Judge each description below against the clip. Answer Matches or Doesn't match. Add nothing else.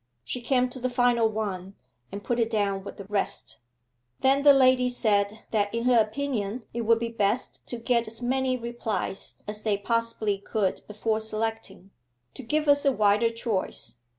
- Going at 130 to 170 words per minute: Doesn't match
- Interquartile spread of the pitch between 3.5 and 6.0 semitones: Doesn't match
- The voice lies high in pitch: Matches